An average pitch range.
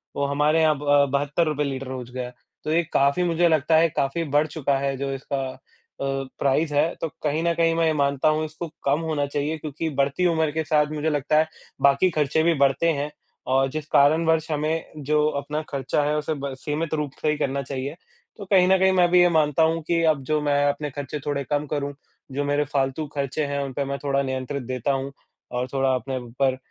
No: narrow, 2.3 semitones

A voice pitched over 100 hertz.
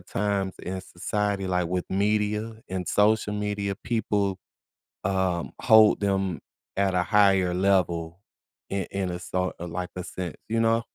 No: very low, 95 Hz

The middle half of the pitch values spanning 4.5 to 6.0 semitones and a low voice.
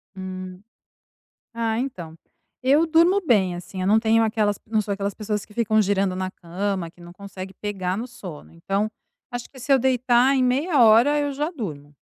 No: average, 5.0 semitones; high, 215 Hz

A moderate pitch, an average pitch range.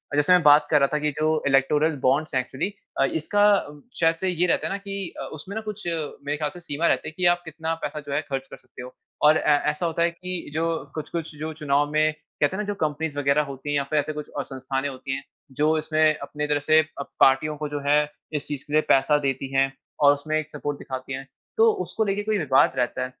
No: medium, 150 Hz; narrow, 2.3 semitones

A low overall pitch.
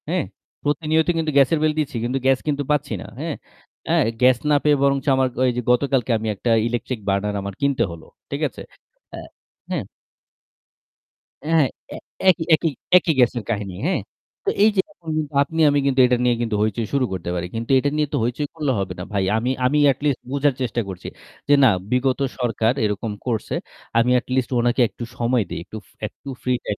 Yes: low, 130 Hz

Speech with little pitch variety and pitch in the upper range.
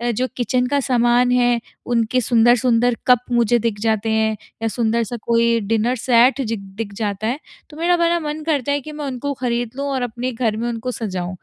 Yes: narrow, 2.2 semitones; high, 240 Hz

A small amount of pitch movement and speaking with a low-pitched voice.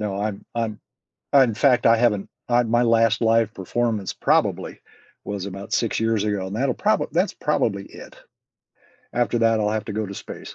Yes: narrow, 2.2 semitones; low, 110 Hz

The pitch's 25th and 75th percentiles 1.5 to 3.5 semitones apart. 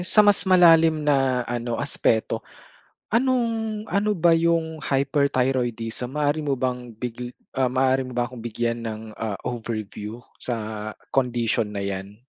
No: average, 5.3 semitones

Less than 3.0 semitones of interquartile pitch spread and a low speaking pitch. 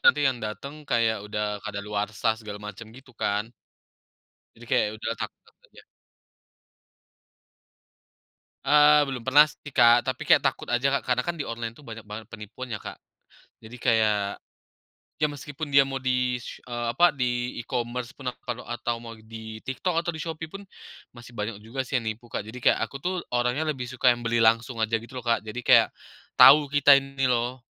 No: average, 3.3 semitones; low, 120 Hz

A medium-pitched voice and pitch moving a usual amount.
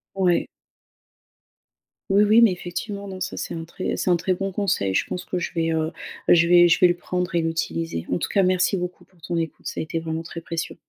No: medium, 175 Hz; narrow, 2.2 semitones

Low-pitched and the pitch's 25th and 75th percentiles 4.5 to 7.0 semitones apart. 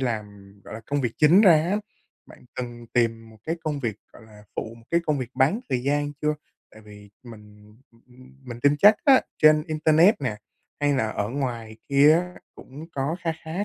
Yes: low, 130 Hz; wide, 5.4 semitones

